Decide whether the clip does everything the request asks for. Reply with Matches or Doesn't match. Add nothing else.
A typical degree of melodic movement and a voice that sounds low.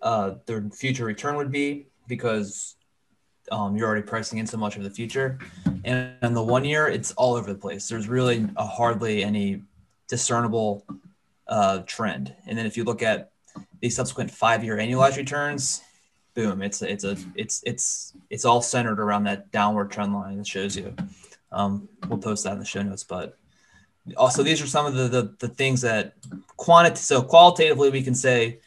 Matches